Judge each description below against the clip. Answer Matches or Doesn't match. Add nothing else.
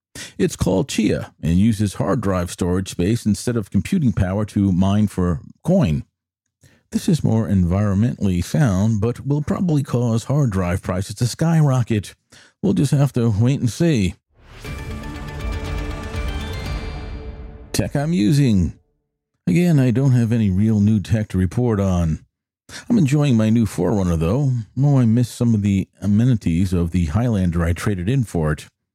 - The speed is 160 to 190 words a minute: Doesn't match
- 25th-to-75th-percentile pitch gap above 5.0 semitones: Matches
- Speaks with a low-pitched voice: Matches